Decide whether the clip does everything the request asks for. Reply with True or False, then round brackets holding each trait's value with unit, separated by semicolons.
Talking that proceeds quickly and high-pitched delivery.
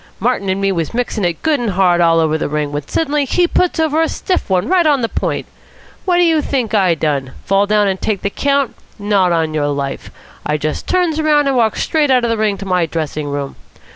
True (240 wpm; 200 Hz)